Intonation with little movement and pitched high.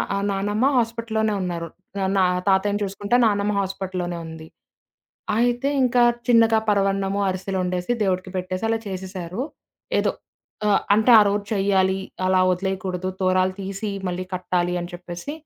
Yes: narrow, 2.1 semitones; high, 195 Hz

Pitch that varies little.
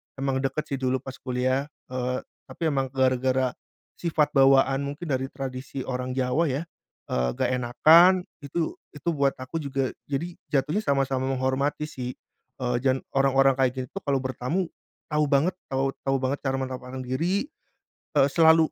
Yes: narrow, 2.1 semitones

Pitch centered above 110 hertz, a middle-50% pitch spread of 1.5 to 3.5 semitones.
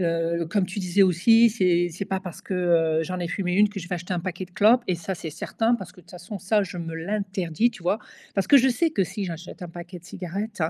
Yes: medium, 185 Hz; average, 2.9 semitones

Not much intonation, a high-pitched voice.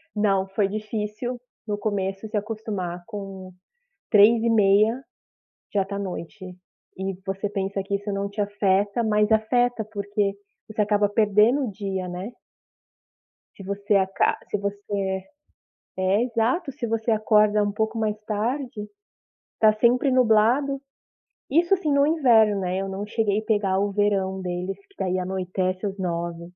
Yes: narrow, 2.2 semitones; high, 205 Hz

